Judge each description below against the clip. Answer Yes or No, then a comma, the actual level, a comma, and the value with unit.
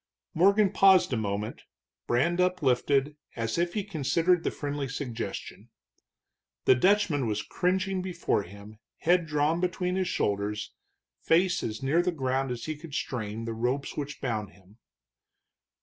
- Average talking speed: Yes, average, 145 wpm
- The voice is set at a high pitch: No, medium, 145 Hz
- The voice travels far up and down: Yes, wide, 7.5 semitones